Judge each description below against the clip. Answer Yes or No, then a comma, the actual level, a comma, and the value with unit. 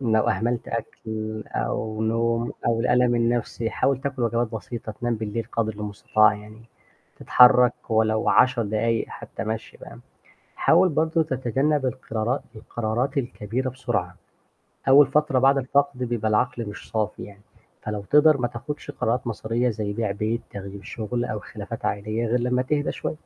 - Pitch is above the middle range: No, low, 115 Hz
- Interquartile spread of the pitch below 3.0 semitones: Yes, narrow, 2.6 semitones